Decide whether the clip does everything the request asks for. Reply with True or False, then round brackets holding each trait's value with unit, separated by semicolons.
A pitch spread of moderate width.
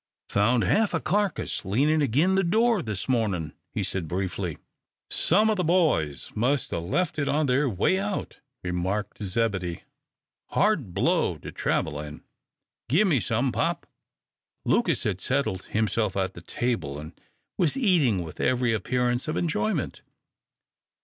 False (8.9 semitones)